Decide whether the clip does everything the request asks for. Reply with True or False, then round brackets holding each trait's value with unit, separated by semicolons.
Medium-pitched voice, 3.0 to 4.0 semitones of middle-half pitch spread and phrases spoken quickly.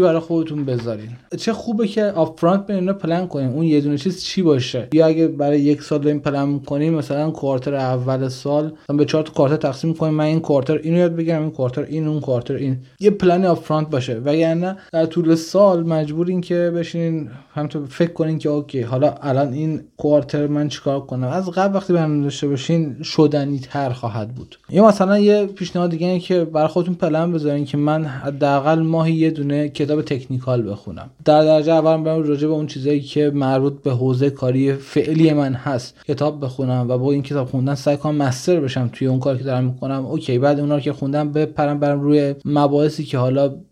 False (150 Hz; 2.6 semitones; 200 wpm)